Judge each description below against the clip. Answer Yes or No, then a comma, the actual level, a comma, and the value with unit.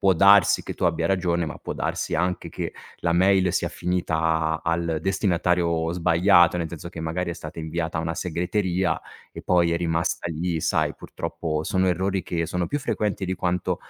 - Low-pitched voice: Yes, very low, 85 Hz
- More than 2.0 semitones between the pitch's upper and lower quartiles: No, narrow, 1.7 semitones